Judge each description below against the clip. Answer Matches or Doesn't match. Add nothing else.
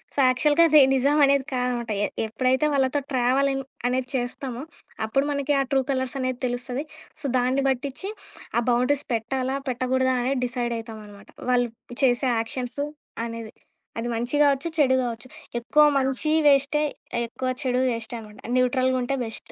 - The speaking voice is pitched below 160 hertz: Doesn't match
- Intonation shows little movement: Matches